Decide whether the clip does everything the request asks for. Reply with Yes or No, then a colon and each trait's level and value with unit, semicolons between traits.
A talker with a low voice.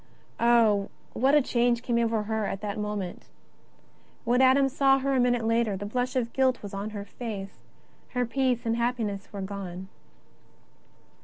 No: high, 230 Hz